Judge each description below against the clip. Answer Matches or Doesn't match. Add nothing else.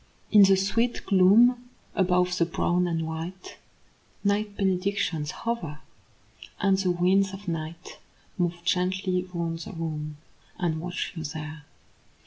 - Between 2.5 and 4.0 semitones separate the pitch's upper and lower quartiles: Matches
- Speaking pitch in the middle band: Matches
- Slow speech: Matches